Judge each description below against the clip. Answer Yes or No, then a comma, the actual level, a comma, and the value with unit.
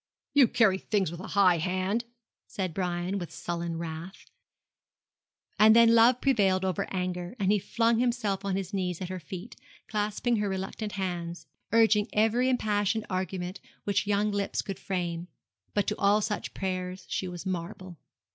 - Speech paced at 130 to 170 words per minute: Yes, average, 160 wpm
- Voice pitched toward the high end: Yes, high, 195 Hz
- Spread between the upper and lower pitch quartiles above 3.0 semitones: No, average, 2.7 semitones